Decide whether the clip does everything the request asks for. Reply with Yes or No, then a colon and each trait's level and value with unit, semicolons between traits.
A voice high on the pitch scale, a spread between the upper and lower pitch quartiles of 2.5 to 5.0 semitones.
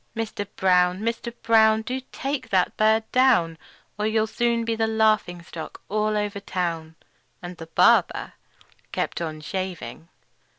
Yes: high, 210 Hz; average, 3.8 semitones